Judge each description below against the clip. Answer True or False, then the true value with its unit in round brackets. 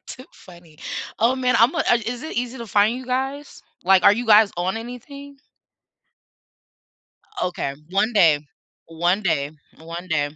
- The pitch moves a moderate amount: False (6.3 semitones)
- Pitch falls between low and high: False (215 Hz)